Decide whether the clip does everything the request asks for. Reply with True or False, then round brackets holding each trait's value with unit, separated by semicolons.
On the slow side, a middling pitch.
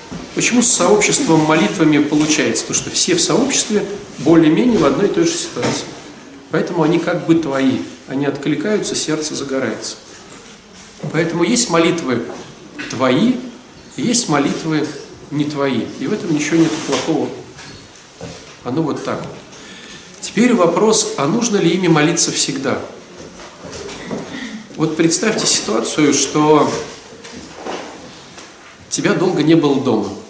False (120 wpm; 165 Hz)